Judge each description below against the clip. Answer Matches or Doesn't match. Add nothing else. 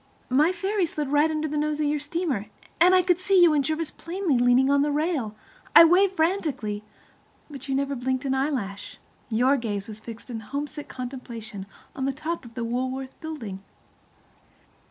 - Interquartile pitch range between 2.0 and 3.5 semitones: Doesn't match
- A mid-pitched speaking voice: Doesn't match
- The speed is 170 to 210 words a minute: Matches